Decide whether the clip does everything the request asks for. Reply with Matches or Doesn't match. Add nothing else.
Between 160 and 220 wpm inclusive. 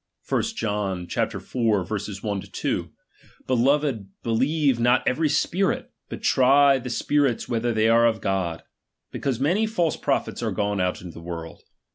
Doesn't match